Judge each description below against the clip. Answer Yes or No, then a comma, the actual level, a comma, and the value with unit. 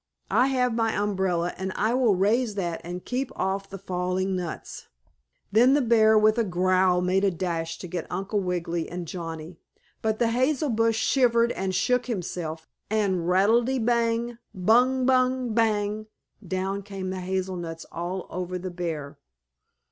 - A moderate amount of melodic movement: Yes, average, 4.2 semitones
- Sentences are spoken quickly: No, average, 165 wpm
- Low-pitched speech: No, high, 195 Hz